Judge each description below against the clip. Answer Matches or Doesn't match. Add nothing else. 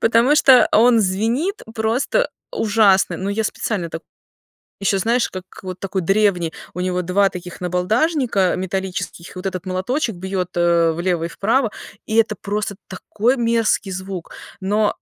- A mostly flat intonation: Doesn't match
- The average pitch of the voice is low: Doesn't match